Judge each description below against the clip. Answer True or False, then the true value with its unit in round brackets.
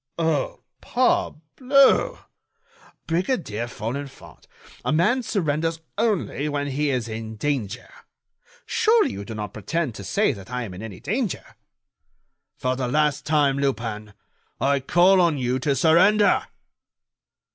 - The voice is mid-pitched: True (145 Hz)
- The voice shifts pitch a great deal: True (6.5 semitones)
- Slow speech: True (125 wpm)